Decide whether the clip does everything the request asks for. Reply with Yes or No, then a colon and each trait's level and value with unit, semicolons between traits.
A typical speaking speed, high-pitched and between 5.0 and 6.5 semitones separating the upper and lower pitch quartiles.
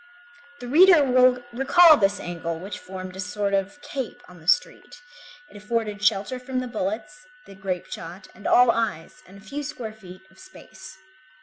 Yes: average, 180 wpm; high, 215 Hz; wide, 5.6 semitones